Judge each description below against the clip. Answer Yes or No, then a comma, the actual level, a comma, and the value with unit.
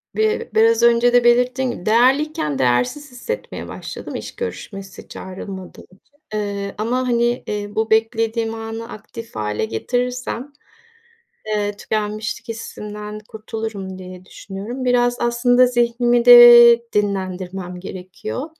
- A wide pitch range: No, average, 3.5 semitones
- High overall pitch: Yes, high, 225 Hz